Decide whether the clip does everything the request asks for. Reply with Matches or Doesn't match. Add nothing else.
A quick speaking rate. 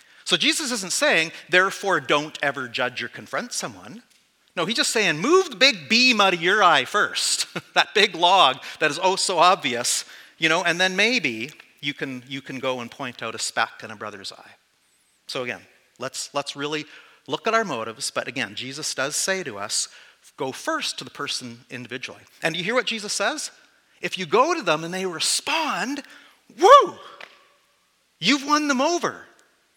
Doesn't match